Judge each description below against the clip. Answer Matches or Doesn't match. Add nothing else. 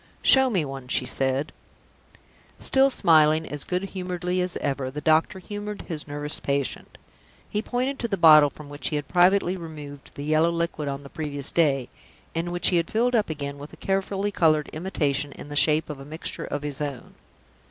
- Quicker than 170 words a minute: Matches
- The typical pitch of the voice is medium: Matches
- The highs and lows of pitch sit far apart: Doesn't match